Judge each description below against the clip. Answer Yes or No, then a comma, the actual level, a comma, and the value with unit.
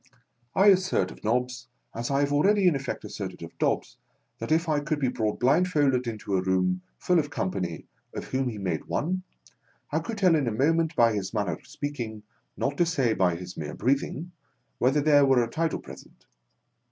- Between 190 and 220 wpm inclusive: Yes, average, 200 wpm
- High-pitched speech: No, low, 130 Hz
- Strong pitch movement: Yes, wide, 6.5 semitones